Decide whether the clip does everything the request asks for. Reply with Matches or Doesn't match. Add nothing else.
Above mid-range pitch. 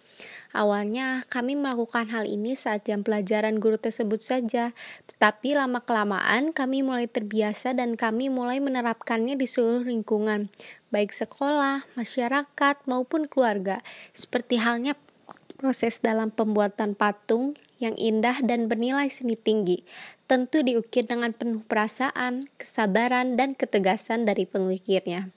Matches